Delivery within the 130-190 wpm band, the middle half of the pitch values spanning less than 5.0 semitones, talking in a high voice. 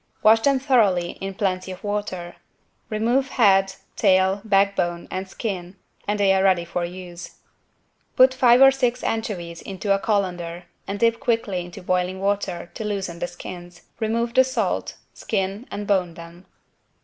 Yes: average, 155 wpm; average, 3.7 semitones; high, 195 Hz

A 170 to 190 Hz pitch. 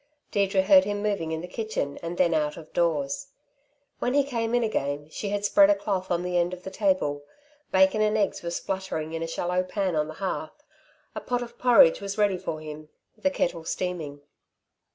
Yes: medium, 185 Hz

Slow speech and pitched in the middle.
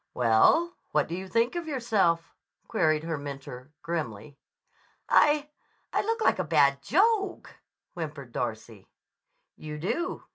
Yes: slow, 130 wpm; medium, 165 Hz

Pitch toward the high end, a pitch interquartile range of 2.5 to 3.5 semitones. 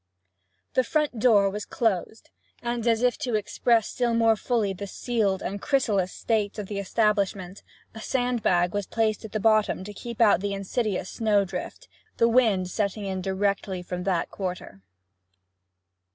Yes: high, 210 Hz; average, 3.1 semitones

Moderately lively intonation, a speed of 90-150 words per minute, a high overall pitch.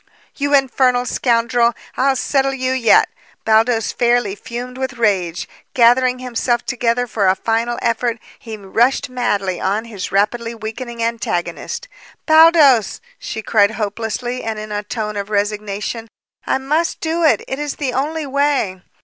Yes: average, 3.4 semitones; average, 145 wpm; high, 235 Hz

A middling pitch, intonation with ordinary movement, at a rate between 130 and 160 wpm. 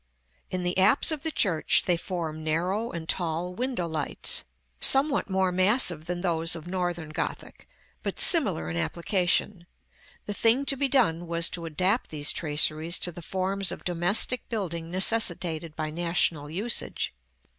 Yes: medium, 175 Hz; average, 3.3 semitones; average, 155 wpm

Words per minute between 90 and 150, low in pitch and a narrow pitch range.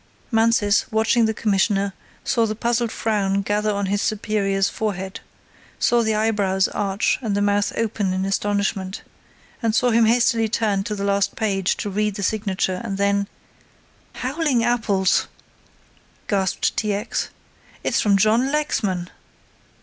No: average, 140 wpm; high, 205 Hz; narrow, 2.2 semitones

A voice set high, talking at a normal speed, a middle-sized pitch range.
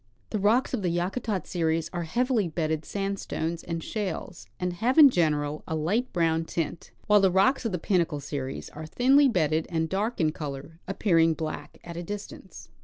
No: medium, 175 Hz; average, 180 wpm; average, 4.4 semitones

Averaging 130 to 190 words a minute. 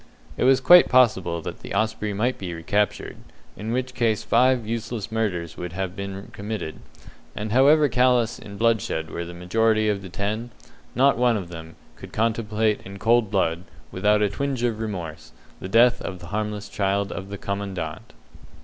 Yes: average, 175 wpm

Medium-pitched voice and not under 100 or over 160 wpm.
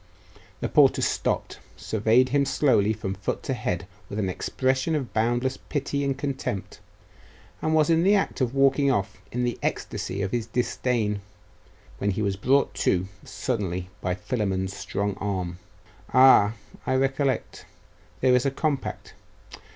No: low, 120 Hz; average, 150 wpm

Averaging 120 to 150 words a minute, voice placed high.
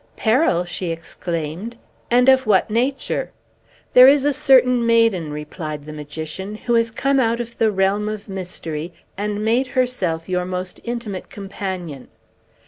Yes: average, 145 wpm; high, 205 Hz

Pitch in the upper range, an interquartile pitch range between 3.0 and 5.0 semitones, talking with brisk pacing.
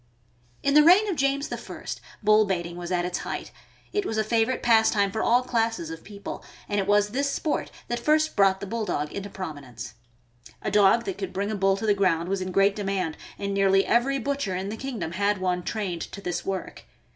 Yes: high, 200 Hz; average, 3.9 semitones; fast, 215 wpm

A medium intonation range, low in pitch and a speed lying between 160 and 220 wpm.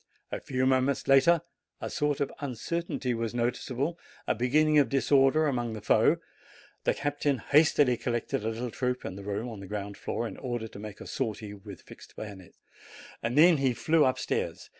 Yes: average, 4.1 semitones; low, 125 Hz; average, 180 wpm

